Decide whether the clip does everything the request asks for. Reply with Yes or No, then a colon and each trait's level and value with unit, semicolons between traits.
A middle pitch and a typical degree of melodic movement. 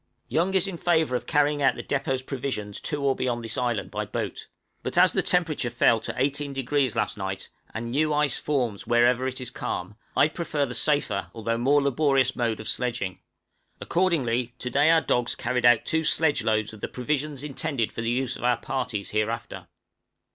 No: low, 130 Hz; average, 3.9 semitones